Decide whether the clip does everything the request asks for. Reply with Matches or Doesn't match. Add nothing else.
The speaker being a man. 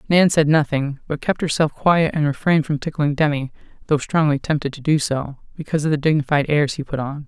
Doesn't match